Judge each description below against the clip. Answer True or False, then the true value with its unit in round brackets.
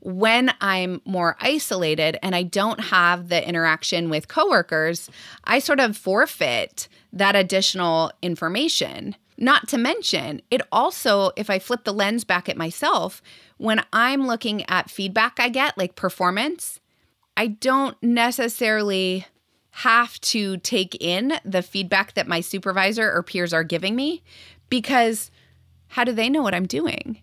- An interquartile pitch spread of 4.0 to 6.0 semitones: True (4.9 semitones)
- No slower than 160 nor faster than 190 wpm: False (145 wpm)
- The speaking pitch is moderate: False (200 Hz)